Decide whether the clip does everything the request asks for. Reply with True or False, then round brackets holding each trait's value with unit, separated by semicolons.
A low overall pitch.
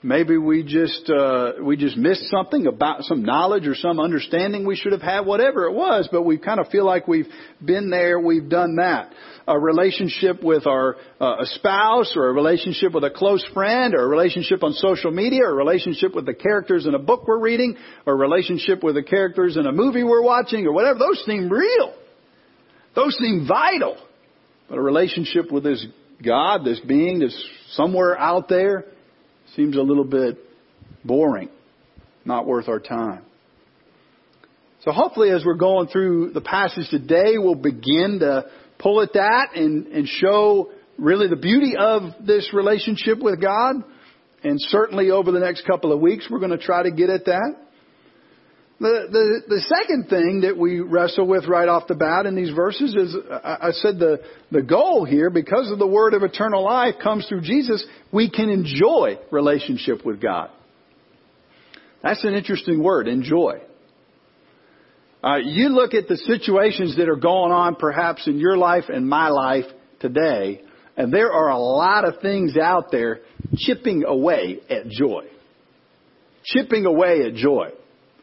False (190 Hz)